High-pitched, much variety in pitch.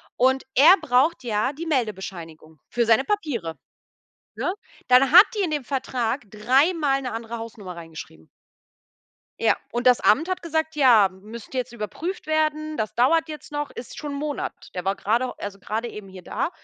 Yes: very high, 250 Hz; wide, 6.1 semitones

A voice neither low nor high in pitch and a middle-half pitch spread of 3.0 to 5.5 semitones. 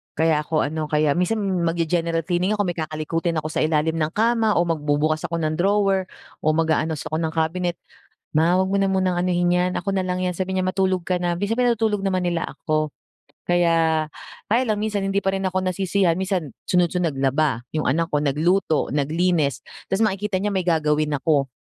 Yes: medium, 175 Hz; average, 3.3 semitones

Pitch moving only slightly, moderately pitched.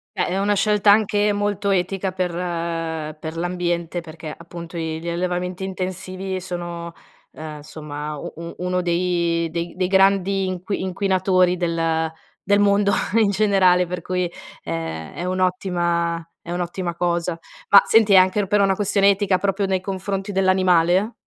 Yes: narrow, 2.2 semitones; medium, 180 Hz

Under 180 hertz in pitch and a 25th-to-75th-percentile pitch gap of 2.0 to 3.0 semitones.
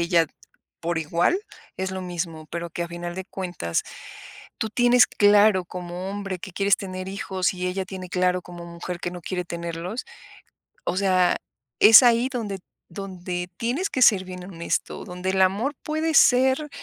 No: medium, 185 Hz; narrow, 2.6 semitones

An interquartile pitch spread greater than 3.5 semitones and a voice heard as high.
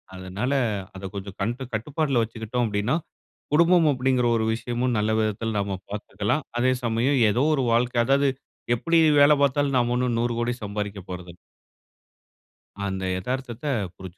No: average, 4.1 semitones; low, 120 Hz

